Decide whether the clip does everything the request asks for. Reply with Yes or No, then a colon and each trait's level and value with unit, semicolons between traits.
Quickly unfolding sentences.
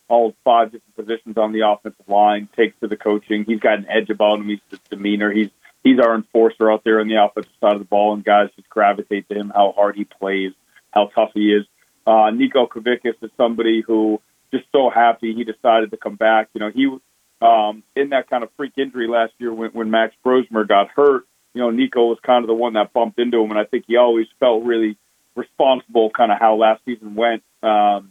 Yes: fast, 230 wpm